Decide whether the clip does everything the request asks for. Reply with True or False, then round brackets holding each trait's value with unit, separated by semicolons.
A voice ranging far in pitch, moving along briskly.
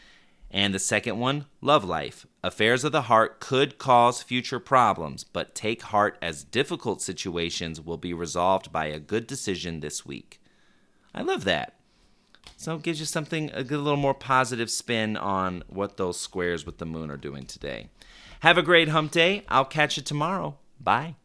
False (9.0 semitones; 175 wpm)